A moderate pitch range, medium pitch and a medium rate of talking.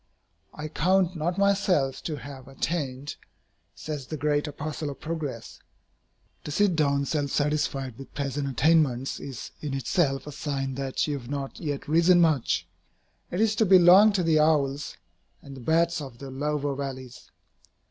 Yes: average, 3.1 semitones; medium, 145 Hz; average, 160 wpm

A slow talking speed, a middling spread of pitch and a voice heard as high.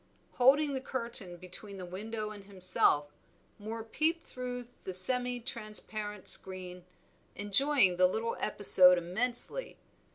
Yes: slow, 120 wpm; average, 5.0 semitones; high, 215 Hz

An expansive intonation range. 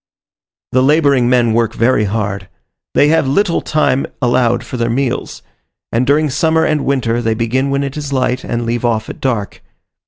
No: average, 3.1 semitones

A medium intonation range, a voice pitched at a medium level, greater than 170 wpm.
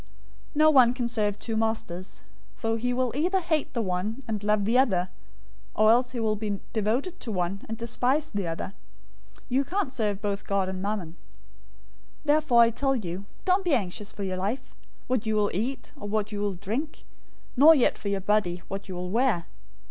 No: average, 4.5 semitones; high, 220 Hz; average, 200 wpm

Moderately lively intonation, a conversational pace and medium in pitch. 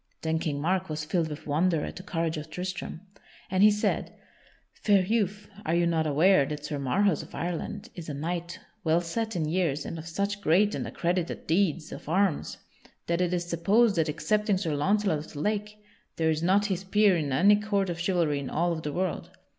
No: average, 3.7 semitones; fast, 210 wpm; medium, 175 Hz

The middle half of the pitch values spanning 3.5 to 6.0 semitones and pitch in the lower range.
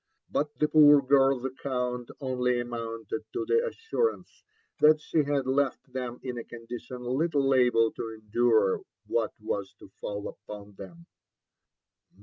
Yes: average, 3.8 semitones; low, 125 Hz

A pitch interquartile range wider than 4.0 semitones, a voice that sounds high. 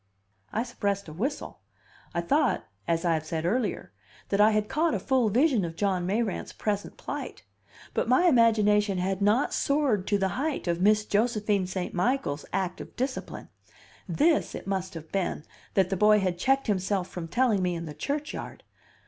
Yes: average, 4.6 semitones; high, 205 Hz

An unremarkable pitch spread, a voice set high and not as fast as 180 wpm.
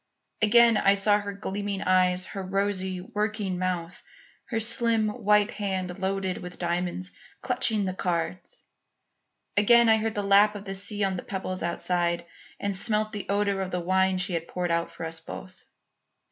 No: narrow, 2.3 semitones; high, 195 Hz; average, 170 wpm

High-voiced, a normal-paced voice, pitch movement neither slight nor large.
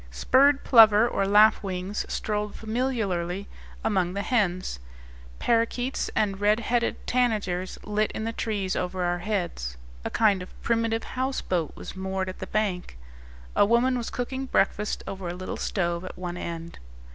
Yes: high, 205 Hz; average, 150 wpm; average, 3.9 semitones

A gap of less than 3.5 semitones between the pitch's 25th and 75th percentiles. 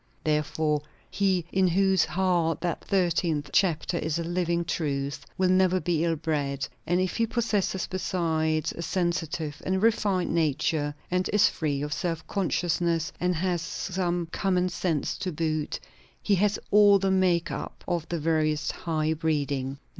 Yes: average, 3.0 semitones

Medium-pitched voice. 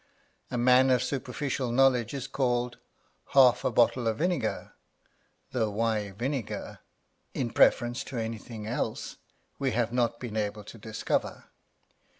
No: low, 120 Hz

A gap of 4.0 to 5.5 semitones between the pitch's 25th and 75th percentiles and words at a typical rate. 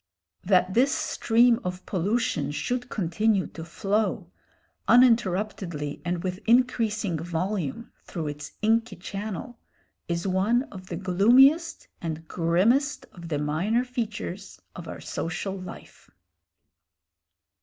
No: average, 5.1 semitones; slow, 110 wpm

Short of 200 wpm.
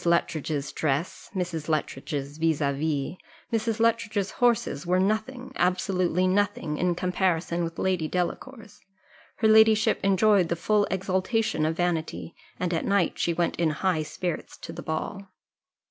Yes: average, 145 wpm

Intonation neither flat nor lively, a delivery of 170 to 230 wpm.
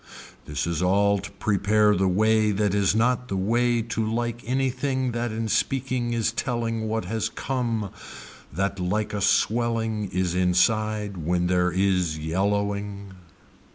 No: average, 3.3 semitones; average, 145 wpm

